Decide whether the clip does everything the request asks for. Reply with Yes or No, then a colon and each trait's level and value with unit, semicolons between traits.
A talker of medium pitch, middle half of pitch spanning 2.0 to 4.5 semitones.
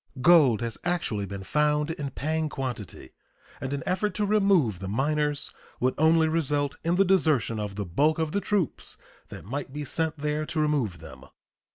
No: medium, 150 Hz; average, 5.1 semitones